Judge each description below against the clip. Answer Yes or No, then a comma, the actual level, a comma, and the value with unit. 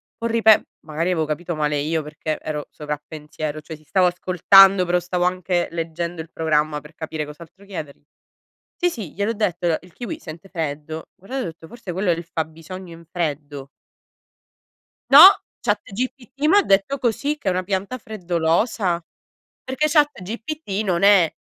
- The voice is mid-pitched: Yes, medium, 175 Hz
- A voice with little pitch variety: No, average, 4.2 semitones